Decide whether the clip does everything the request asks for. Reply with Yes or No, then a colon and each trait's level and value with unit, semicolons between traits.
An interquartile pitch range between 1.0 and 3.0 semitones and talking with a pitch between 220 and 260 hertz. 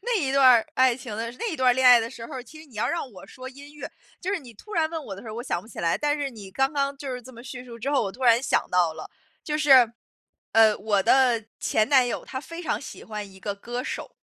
No: average, 3.9 semitones; very high, 250 Hz